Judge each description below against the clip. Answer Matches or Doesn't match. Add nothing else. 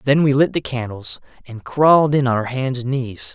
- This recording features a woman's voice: Doesn't match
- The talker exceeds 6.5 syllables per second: Doesn't match